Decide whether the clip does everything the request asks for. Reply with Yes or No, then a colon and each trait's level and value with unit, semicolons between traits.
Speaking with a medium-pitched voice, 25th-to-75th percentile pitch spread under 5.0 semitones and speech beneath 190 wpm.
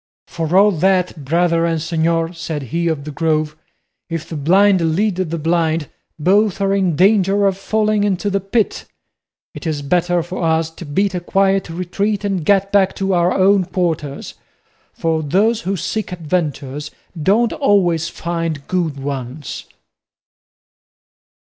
Yes: medium, 175 Hz; average, 3.4 semitones; average, 150 wpm